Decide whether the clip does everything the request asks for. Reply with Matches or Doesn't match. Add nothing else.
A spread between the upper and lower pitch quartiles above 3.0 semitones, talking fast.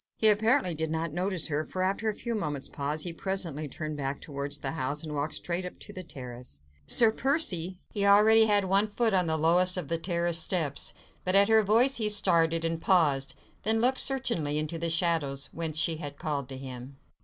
Matches